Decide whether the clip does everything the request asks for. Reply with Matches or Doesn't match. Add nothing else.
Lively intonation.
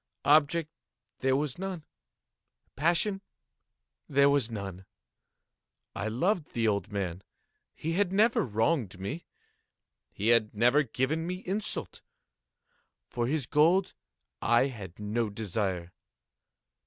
Matches